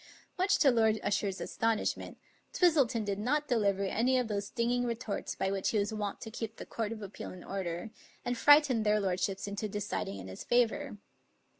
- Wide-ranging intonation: No, average, 3.4 semitones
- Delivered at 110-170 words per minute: No, average, 185 wpm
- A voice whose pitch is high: Yes, high, 220 Hz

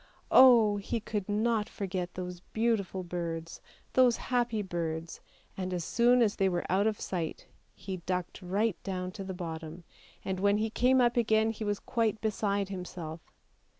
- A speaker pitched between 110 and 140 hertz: No, high, 200 Hz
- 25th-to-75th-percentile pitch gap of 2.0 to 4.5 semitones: Yes, average, 3.5 semitones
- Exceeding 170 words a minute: No, average, 165 wpm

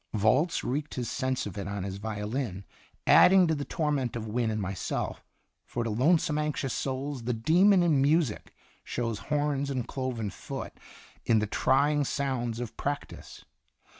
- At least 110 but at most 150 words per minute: No, average, 165 wpm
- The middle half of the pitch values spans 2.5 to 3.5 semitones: No, average, 4.9 semitones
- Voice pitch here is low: Yes, low, 130 Hz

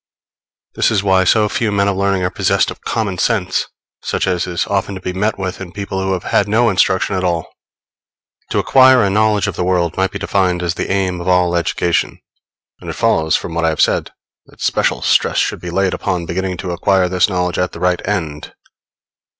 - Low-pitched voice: Yes, very low, 95 Hz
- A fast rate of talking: Yes, fast, 215 wpm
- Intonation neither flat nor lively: No, narrow, 1.9 semitones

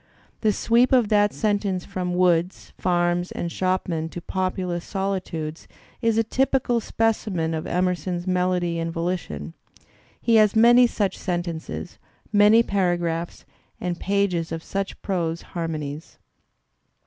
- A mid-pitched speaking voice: Yes, medium, 180 Hz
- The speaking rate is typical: No, slow, 125 wpm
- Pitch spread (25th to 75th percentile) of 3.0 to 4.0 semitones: Yes, average, 3.3 semitones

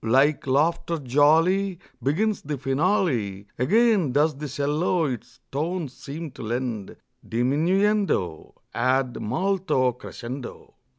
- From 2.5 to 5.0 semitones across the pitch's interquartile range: No, wide, 5.6 semitones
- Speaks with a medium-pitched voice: Yes, medium, 145 Hz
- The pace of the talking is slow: Yes, slow, 105 wpm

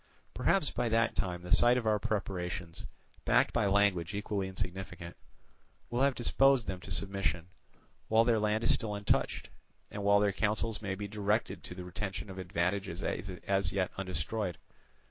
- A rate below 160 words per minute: No, average, 165 wpm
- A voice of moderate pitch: No, low, 100 Hz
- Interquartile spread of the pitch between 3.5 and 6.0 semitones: No, average, 2.8 semitones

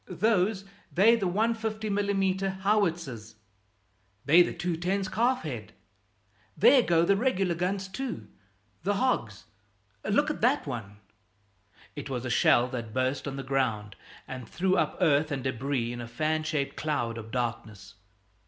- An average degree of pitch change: No, wide, 7.9 semitones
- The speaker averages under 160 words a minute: Yes, average, 145 wpm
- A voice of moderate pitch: Yes, medium, 165 Hz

